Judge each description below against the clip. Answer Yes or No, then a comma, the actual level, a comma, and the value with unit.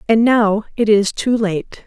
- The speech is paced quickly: No, average, 195 wpm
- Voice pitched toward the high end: Yes, high, 215 Hz